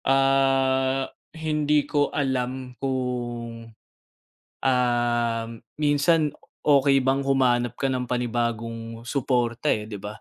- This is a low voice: Yes, low, 130 Hz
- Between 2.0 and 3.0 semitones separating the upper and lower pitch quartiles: Yes, narrow, 2.4 semitones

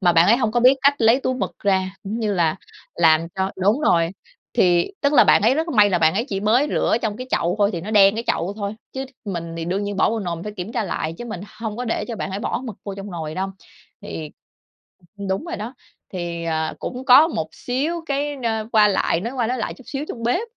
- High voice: Yes, high, 210 Hz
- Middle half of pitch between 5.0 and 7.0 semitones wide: Yes, wide, 5.4 semitones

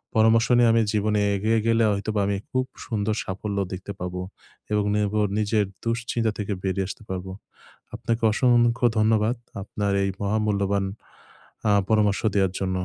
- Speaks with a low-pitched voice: Yes, low, 105 Hz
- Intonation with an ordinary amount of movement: No, narrow, 2.2 semitones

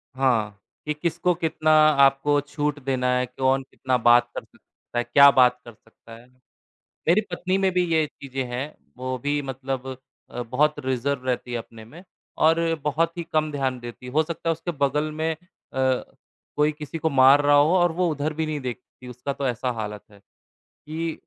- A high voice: No, medium, 140 Hz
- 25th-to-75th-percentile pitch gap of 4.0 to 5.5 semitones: No, average, 3.6 semitones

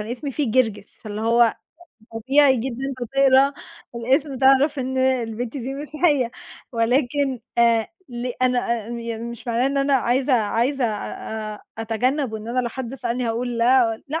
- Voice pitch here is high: Yes, high, 245 Hz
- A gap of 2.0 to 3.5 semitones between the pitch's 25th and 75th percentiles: Yes, average, 2.7 semitones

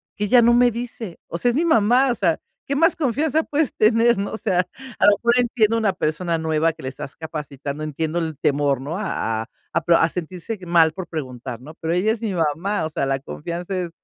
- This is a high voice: No, medium, 180 Hz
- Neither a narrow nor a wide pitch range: No, wide, 6.8 semitones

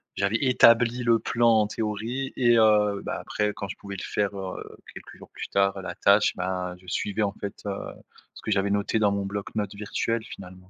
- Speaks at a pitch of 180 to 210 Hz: No, low, 105 Hz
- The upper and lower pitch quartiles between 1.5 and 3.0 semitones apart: Yes, narrow, 2.4 semitones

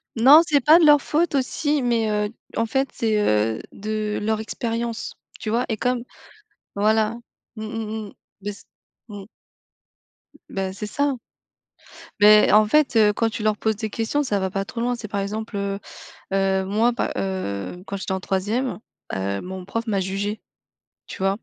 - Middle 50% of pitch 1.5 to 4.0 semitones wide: Yes, average, 2.9 semitones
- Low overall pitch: No, high, 215 Hz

